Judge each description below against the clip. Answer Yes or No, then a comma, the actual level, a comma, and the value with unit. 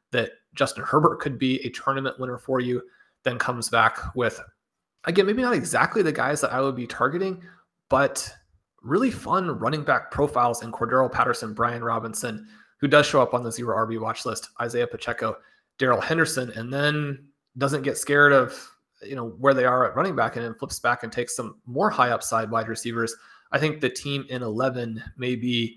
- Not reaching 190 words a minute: No, average, 195 wpm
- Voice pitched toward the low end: Yes, low, 125 Hz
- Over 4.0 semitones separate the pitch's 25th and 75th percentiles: No, average, 3.3 semitones